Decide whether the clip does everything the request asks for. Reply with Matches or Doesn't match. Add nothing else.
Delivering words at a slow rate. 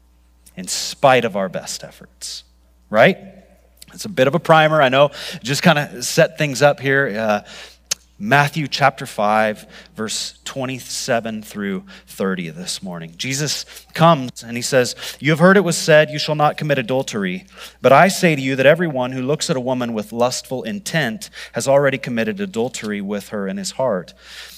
Doesn't match